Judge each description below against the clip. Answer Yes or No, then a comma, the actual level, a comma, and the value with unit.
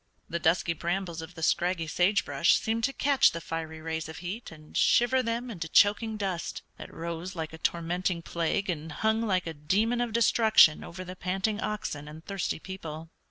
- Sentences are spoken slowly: No, average, 190 wpm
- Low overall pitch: No, medium, 175 Hz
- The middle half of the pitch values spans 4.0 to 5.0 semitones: Yes, average, 4.6 semitones